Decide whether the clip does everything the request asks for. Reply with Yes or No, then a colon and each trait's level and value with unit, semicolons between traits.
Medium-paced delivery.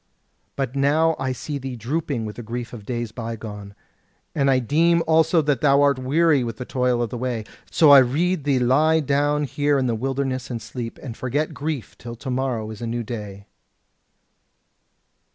Yes: average, 190 wpm